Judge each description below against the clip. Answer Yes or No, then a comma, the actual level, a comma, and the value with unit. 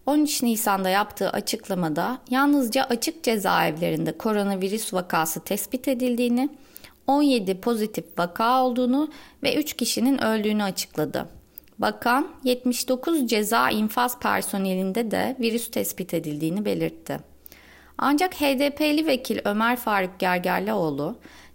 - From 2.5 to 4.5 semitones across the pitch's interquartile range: No, average, 5.3 semitones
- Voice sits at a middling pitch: No, high, 230 Hz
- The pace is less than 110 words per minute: Yes, average, 100 wpm